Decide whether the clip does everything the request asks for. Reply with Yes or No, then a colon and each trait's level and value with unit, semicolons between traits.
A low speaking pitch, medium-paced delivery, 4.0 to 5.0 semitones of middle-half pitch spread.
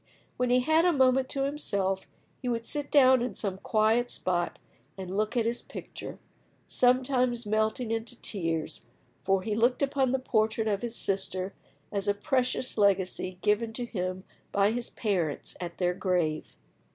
No: high, 220 Hz; average, 165 wpm; average, 4.5 semitones